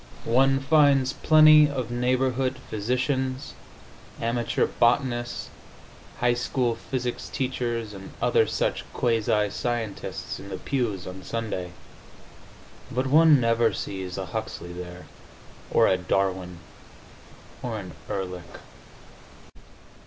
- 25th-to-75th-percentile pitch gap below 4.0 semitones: No, average, 5.0 semitones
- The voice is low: Yes, low, 120 Hz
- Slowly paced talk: Yes, slow, 105 wpm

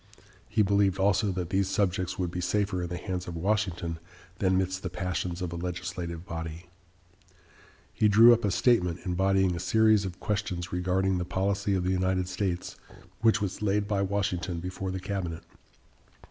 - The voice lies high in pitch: No, very low, 95 Hz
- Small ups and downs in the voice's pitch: Yes, narrow, 2.1 semitones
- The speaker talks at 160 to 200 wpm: Yes, average, 175 wpm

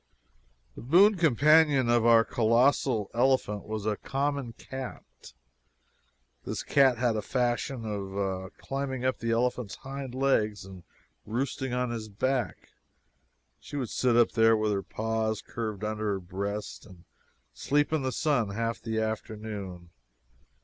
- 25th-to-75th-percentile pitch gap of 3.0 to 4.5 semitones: Yes, average, 3.7 semitones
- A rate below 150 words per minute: Yes, average, 140 wpm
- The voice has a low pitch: Yes, low, 115 Hz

